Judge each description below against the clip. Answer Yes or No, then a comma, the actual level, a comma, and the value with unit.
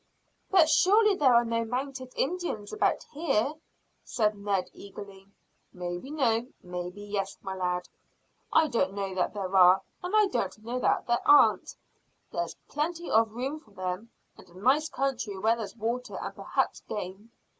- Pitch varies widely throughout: Yes, wide, 6.0 semitones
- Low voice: No, high, 230 Hz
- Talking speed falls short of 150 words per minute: No, average, 160 wpm